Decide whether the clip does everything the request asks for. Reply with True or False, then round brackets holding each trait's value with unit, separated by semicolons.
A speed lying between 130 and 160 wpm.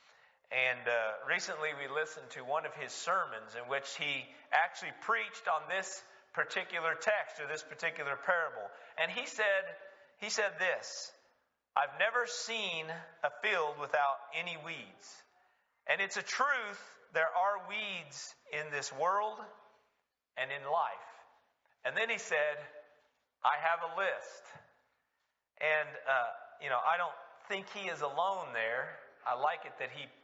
True (145 wpm)